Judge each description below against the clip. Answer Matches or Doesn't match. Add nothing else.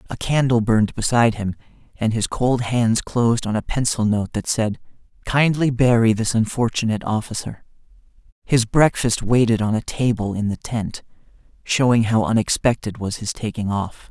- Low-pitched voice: Matches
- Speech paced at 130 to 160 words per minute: Matches